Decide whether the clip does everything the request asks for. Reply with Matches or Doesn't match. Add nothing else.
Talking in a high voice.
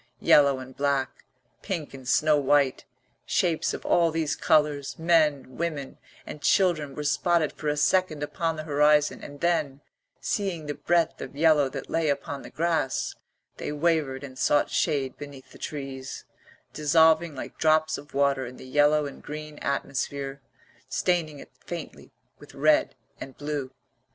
Doesn't match